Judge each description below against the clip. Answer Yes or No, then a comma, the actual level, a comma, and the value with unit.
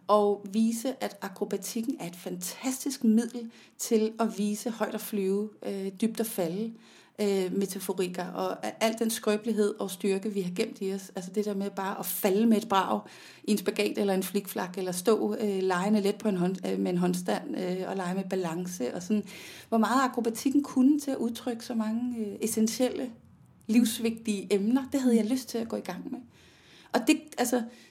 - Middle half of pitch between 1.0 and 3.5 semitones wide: Yes, average, 3.0 semitones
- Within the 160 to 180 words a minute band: No, average, 200 wpm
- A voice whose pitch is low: No, high, 210 Hz